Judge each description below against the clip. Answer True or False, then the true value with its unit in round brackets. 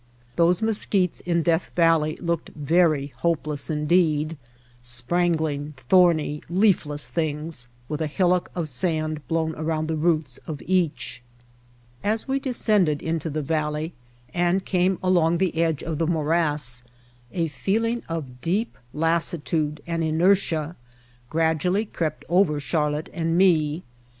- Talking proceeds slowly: True (130 wpm)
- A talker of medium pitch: True (165 Hz)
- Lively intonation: False (2.6 semitones)